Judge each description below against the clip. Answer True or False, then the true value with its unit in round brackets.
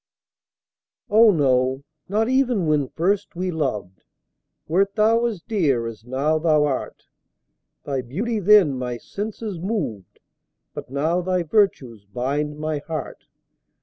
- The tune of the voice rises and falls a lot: True (7.3 semitones)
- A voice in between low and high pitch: True (155 Hz)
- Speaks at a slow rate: True (125 wpm)